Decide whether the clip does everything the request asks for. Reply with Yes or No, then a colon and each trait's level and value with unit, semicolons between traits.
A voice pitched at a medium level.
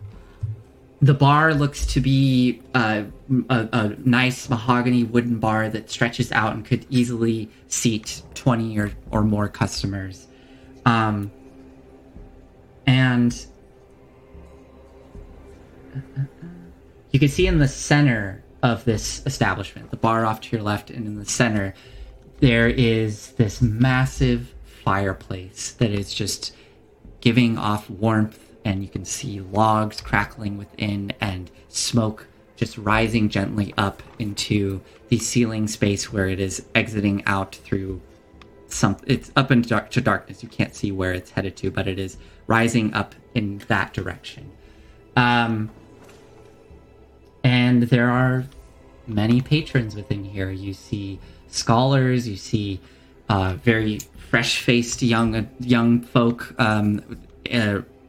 No: low, 110 Hz